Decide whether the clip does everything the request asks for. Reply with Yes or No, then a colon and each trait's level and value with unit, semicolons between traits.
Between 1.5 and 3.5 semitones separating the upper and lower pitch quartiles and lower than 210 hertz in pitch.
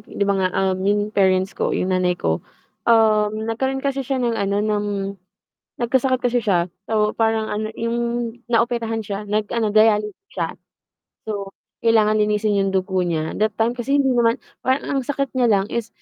No: average, 3.0 semitones; high, 215 Hz